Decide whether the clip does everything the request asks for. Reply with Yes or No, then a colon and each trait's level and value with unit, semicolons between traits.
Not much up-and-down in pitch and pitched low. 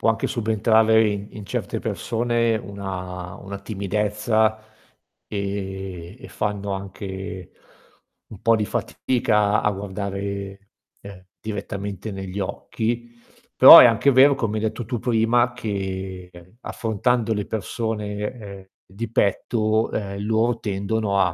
Yes: narrow, 2.3 semitones; low, 105 Hz